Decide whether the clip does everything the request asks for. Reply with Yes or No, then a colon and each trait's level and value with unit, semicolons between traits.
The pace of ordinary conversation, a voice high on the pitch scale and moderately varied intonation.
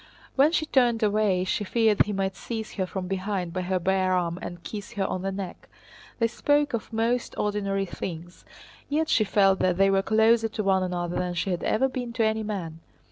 No: fast, 210 wpm; high, 195 Hz; average, 3.3 semitones